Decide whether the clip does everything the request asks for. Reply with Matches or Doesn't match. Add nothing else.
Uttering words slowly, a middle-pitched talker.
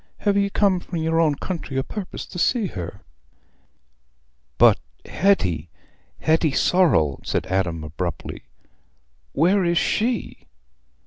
Matches